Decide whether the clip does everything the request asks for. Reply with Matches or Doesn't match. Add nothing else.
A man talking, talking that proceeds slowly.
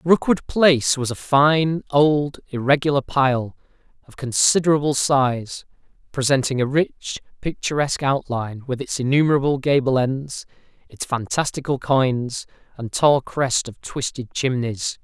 Matches